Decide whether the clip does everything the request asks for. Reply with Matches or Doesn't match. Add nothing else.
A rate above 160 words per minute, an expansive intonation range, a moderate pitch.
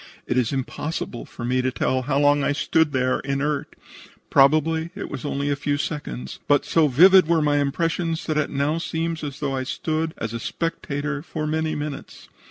Doesn't match